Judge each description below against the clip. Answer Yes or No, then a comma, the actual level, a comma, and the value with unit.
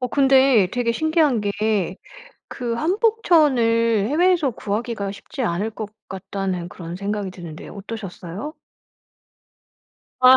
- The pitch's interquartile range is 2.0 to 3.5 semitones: No, average, 5.3 semitones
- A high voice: Yes, high, 225 Hz